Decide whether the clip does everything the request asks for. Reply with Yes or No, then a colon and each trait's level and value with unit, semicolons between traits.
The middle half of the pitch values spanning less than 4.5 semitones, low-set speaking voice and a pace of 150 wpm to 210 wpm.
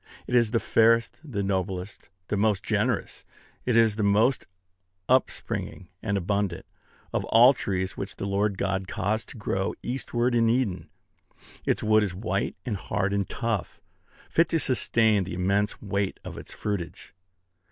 Yes: average, 2.9 semitones; low, 105 Hz; average, 155 wpm